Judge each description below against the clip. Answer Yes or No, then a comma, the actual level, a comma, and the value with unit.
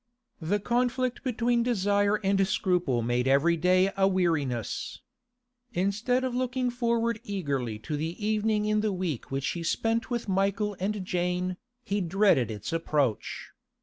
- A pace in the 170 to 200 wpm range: No, average, 145 wpm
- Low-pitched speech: No, high, 195 Hz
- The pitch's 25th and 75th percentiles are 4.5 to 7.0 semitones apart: Yes, average, 5.2 semitones